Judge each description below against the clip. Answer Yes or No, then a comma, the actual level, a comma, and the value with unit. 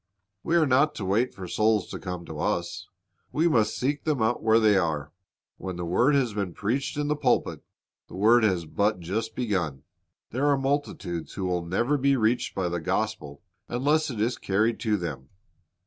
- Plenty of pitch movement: Yes, wide, 6.2 semitones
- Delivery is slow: No, average, 195 wpm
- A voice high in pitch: No, low, 110 Hz